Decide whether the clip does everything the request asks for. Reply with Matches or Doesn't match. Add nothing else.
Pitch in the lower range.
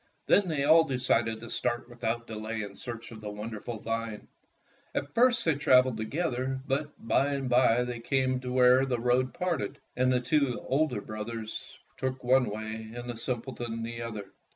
Matches